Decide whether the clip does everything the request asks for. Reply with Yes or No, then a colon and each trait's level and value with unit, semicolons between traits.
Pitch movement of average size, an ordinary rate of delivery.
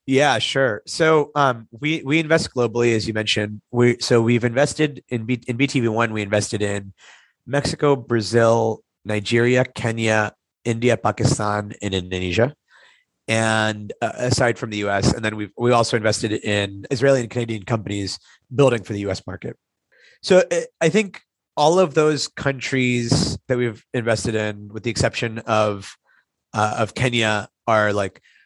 Yes: average, 3.3 semitones; average, 150 wpm